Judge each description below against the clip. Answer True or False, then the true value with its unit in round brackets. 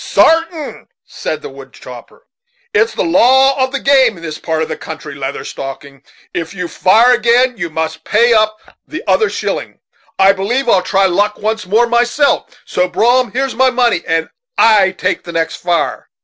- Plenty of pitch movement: True (6.7 semitones)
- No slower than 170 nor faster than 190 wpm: True (180 wpm)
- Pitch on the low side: False (215 Hz)